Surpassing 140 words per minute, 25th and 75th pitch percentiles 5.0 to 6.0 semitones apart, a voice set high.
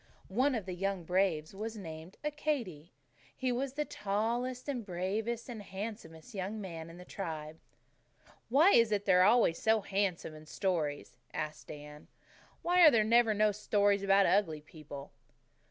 Yes: average, 160 wpm; wide, 5.5 semitones; high, 200 Hz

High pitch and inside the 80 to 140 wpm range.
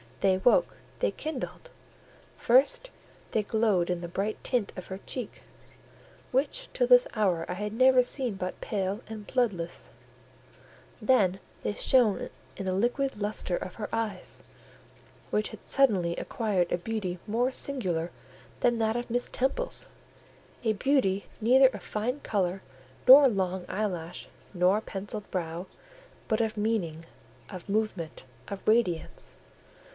Yes: high, 215 Hz; slow, 135 wpm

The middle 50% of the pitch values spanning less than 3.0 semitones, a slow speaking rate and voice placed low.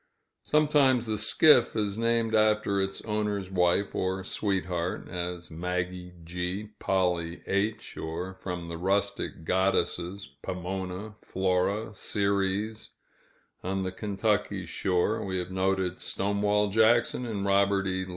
Yes: narrow, 2.6 semitones; slow, 120 wpm; very low, 95 Hz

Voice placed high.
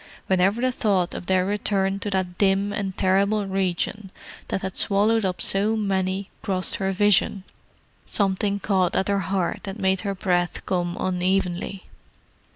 Yes: high, 195 Hz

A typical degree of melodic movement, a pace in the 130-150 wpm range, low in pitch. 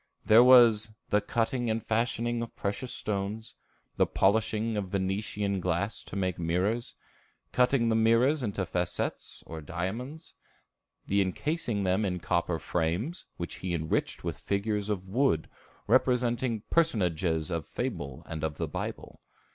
Yes: average, 4.4 semitones; average, 140 wpm; low, 105 Hz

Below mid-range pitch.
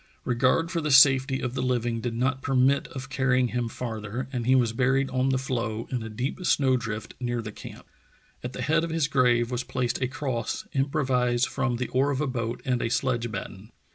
Yes: low, 125 Hz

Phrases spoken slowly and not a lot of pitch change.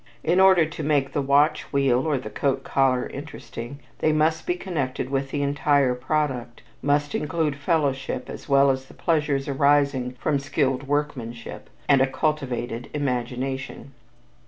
No: average, 150 wpm; narrow, 2.2 semitones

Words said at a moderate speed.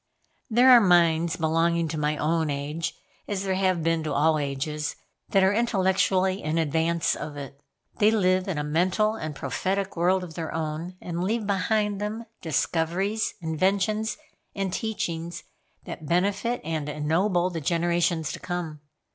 Yes: average, 155 wpm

